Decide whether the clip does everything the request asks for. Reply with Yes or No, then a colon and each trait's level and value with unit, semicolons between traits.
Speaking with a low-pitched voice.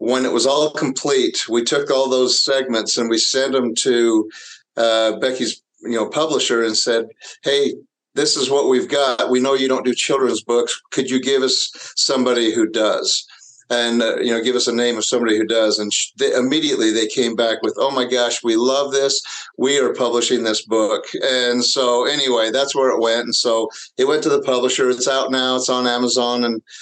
Yes: low, 125 Hz